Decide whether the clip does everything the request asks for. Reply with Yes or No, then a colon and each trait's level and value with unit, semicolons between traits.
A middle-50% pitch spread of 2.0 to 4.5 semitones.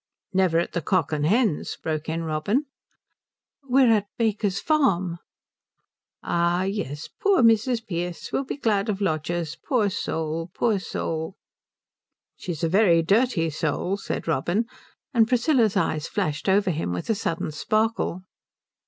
No: average, 5.3 semitones